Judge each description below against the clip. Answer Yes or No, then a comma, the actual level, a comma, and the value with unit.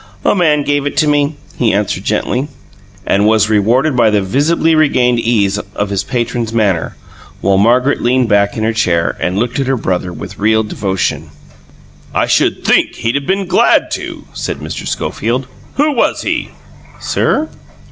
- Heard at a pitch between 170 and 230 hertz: No, low, 115 Hz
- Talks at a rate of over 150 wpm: Yes, average, 170 wpm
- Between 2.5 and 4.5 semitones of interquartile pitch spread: No, wide, 5.4 semitones